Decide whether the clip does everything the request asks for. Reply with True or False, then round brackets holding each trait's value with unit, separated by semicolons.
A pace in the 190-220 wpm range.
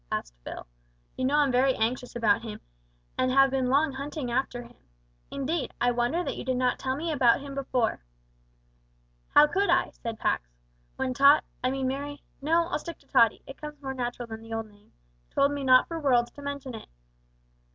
True (200 wpm)